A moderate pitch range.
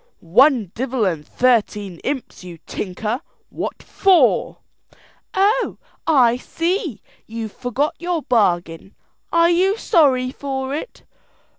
No: wide, 7.5 semitones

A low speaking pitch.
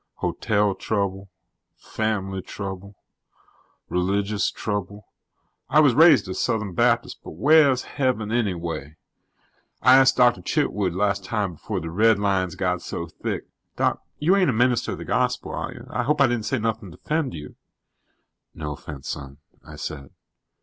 Yes: low, 105 Hz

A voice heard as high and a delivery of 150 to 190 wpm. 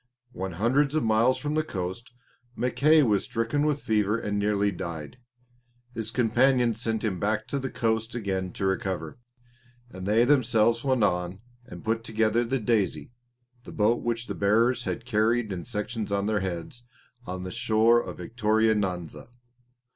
No: low, 110 Hz; average, 160 wpm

